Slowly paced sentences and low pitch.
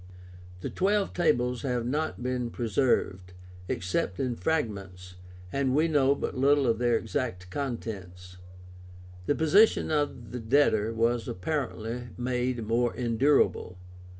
Yes: slow, 125 wpm; low, 125 Hz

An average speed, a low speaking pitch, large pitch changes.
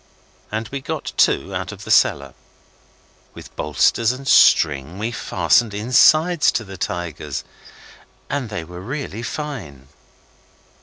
No: slow, 125 wpm; low, 105 Hz; wide, 7.0 semitones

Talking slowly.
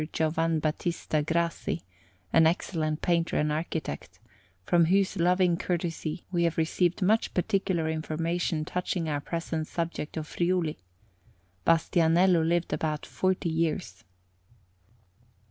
Yes: slow, 110 wpm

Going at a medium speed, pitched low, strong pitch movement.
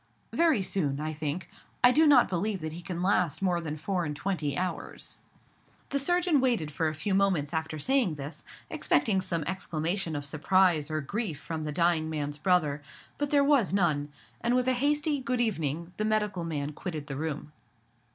No: average, 185 wpm; medium, 175 Hz; wide, 5.8 semitones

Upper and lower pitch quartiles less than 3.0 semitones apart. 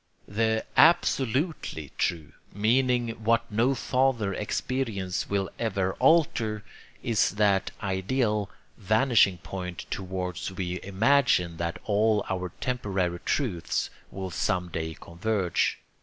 No: average, 4.1 semitones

